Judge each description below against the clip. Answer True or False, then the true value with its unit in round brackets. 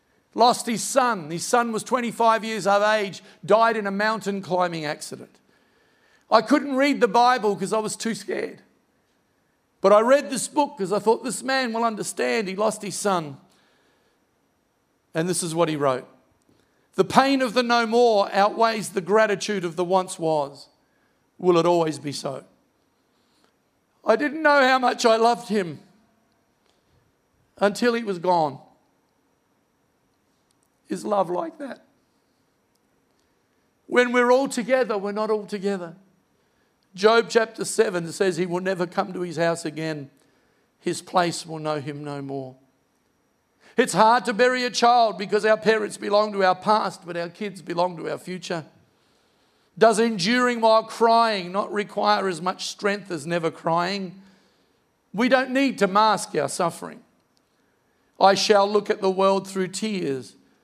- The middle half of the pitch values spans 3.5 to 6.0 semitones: True (4.3 semitones)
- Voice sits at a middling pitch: False (205 Hz)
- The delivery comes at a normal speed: True (155 wpm)